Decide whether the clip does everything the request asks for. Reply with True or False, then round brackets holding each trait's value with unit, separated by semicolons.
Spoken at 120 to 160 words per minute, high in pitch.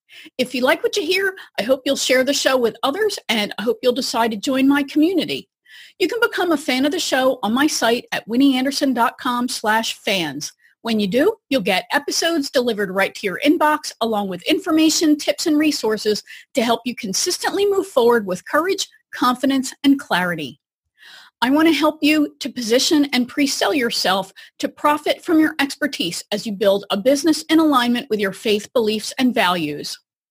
False (185 wpm; 270 Hz)